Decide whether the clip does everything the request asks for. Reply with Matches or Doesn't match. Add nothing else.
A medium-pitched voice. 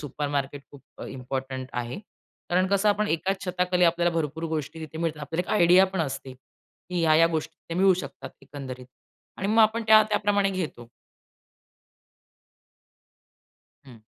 Matches